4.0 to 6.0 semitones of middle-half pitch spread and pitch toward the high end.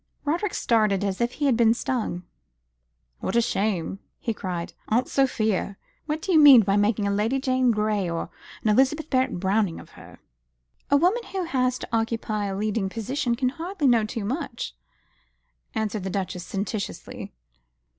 Yes: average, 4.6 semitones; high, 225 Hz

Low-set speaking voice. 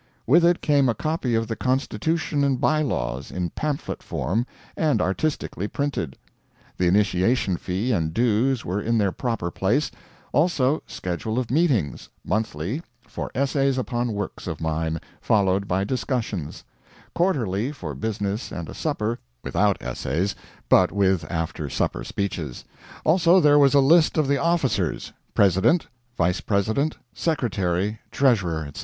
Yes: low, 110 Hz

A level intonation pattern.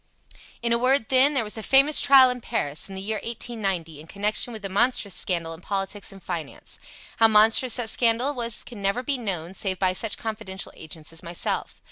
No: average, 4.2 semitones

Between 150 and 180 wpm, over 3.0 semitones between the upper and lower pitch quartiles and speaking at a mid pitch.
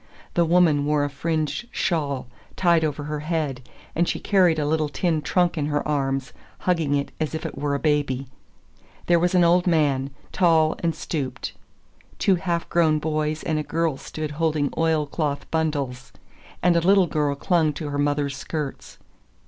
No: average, 175 wpm; narrow, 2.6 semitones; medium, 155 Hz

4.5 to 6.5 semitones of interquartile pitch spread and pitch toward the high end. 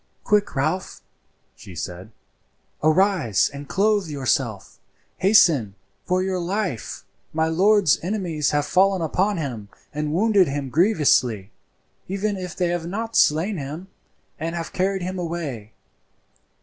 No: average, 5.2 semitones; medium, 170 Hz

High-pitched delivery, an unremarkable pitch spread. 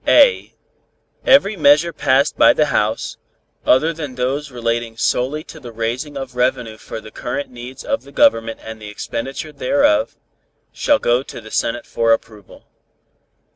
No: low, 130 Hz; average, 4.8 semitones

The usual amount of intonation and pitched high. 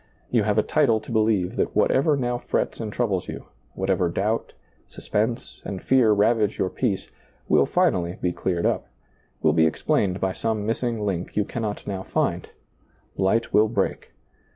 No: average, 3.3 semitones; low, 105 Hz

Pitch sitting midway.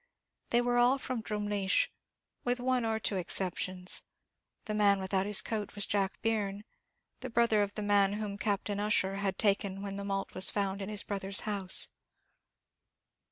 No: high, 205 Hz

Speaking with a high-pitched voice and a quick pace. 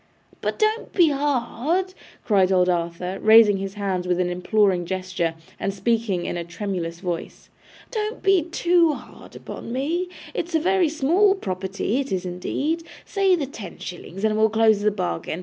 No: high, 215 Hz; average, 165 wpm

